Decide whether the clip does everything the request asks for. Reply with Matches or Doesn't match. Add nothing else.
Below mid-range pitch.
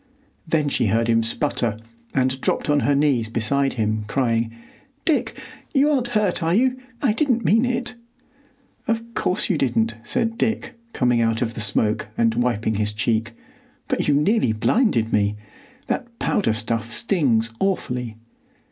Matches